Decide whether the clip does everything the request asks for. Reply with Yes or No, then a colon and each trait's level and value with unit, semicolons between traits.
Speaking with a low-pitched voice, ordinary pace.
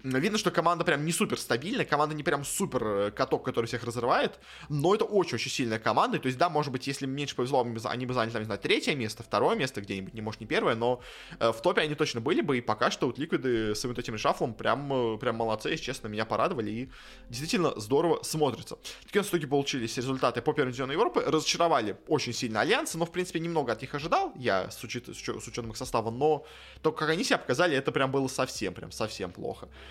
No: low, 130 Hz; fast, 220 wpm